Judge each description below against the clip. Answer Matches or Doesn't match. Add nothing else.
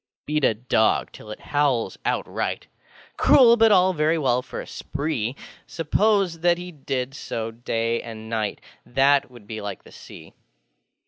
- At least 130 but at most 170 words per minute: Matches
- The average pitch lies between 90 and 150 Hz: Matches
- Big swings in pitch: Matches